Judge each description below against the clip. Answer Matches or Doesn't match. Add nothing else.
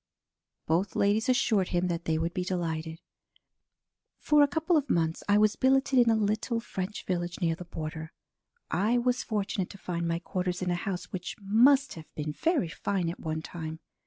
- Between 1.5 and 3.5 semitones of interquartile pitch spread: Doesn't match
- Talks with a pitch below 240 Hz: Matches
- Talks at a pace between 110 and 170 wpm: Doesn't match